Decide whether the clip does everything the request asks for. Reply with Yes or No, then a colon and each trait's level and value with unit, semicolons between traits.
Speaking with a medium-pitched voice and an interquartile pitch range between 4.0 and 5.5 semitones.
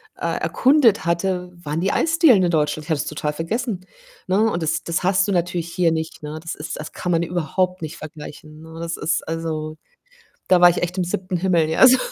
No: medium, 170 Hz; average, 2.7 semitones